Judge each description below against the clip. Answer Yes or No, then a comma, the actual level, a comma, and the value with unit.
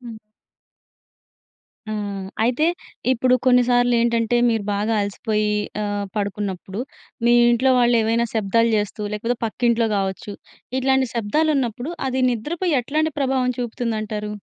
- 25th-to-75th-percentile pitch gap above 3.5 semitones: No, average, 2.9 semitones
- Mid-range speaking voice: No, high, 235 Hz